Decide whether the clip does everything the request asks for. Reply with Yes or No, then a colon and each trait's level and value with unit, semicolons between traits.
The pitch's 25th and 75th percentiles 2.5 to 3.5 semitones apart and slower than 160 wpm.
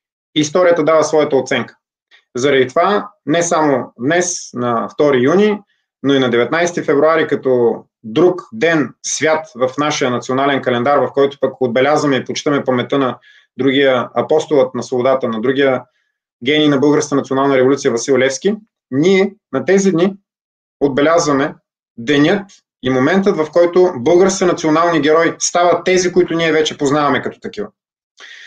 No: average, 4.7 semitones; average, 140 wpm